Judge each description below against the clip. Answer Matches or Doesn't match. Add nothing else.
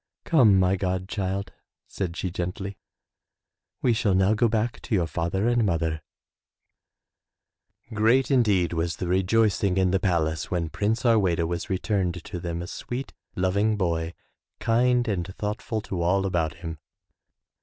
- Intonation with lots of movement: Doesn't match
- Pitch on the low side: Matches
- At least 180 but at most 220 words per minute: Doesn't match